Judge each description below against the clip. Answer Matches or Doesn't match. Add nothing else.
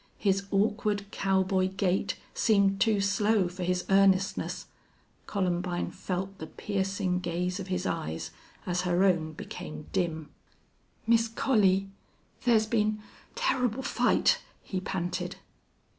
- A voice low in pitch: Doesn't match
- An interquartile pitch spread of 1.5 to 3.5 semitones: Matches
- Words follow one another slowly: Matches